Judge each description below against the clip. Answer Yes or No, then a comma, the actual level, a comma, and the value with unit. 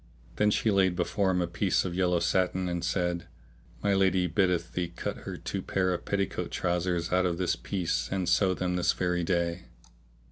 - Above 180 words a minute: Yes, average, 190 wpm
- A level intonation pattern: Yes, narrow, 1.4 semitones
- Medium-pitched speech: No, very low, 90 Hz